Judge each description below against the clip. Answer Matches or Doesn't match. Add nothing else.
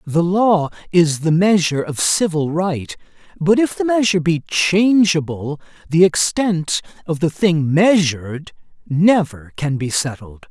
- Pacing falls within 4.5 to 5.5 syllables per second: Doesn't match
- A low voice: Doesn't match